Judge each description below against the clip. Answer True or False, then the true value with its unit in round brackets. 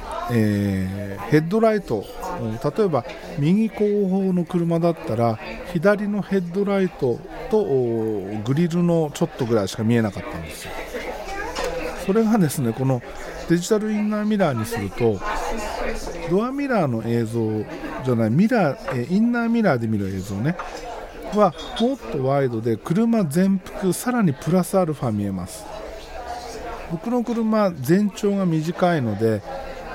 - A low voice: False (170 Hz)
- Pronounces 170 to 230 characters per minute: False (280 characters per minute)